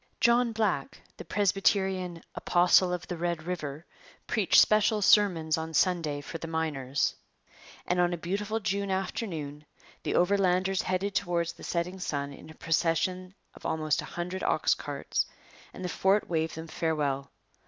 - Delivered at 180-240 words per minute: No, average, 155 wpm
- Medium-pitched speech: Yes, medium, 175 Hz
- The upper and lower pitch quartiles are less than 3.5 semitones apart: Yes, average, 3.1 semitones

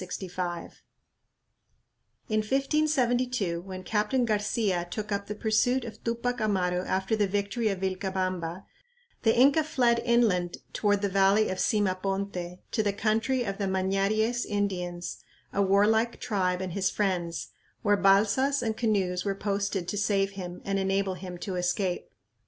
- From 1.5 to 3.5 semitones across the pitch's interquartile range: Yes, average, 2.9 semitones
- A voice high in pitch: Yes, high, 200 Hz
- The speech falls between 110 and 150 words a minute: Yes, average, 145 wpm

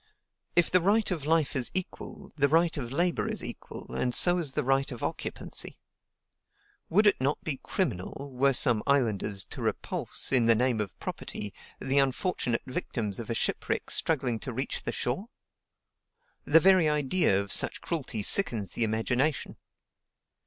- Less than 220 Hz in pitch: Yes, low, 135 Hz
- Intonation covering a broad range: Yes, wide, 5.8 semitones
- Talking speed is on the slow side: No, average, 160 wpm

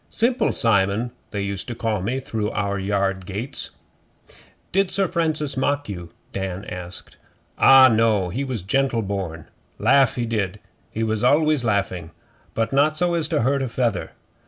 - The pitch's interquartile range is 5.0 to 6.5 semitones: Yes, wide, 5.6 semitones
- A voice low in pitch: Yes, low, 115 Hz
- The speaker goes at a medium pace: Yes, average, 160 wpm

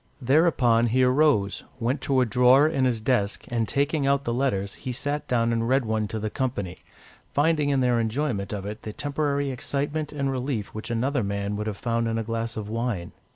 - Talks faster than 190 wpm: Yes, fast, 205 wpm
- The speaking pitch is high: No, low, 125 Hz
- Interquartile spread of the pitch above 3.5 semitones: Yes, average, 4.0 semitones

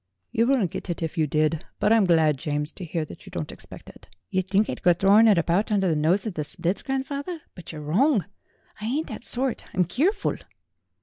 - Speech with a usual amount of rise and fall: No, wide, 6.0 semitones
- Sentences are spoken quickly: Yes, fast, 225 wpm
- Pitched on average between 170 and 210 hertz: Yes, high, 190 Hz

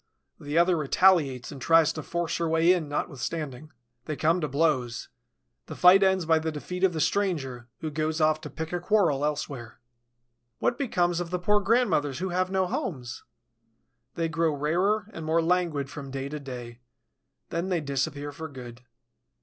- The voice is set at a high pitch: No, medium, 160 Hz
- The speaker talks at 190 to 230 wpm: No, average, 175 wpm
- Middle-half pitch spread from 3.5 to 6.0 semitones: Yes, average, 3.8 semitones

